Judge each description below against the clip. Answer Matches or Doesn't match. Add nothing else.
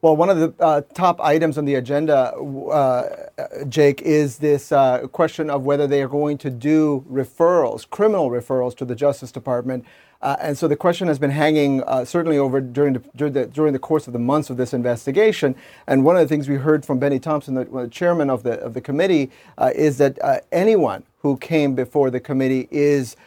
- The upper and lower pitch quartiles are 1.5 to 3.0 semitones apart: Matches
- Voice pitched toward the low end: Doesn't match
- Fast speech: Matches